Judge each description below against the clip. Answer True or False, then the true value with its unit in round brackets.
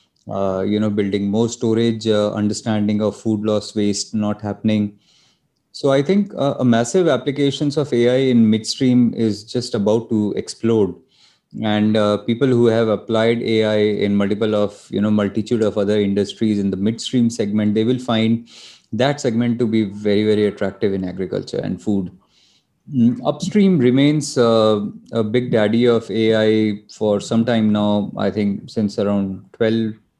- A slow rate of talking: False (165 wpm)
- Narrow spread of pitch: True (2.3 semitones)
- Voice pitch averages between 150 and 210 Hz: False (110 Hz)